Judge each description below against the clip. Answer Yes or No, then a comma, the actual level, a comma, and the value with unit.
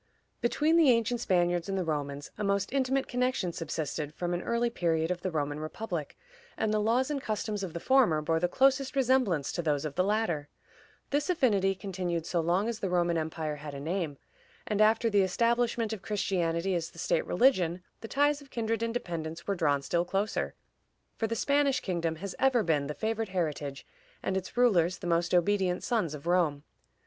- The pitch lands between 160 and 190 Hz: Yes, medium, 185 Hz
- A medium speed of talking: Yes, average, 195 wpm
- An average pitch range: No, wide, 5.7 semitones